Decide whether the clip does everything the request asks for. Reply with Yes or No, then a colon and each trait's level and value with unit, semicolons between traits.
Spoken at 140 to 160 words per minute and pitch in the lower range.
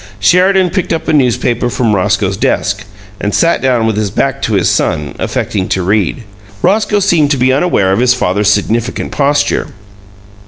No: average, 170 wpm; low, 120 Hz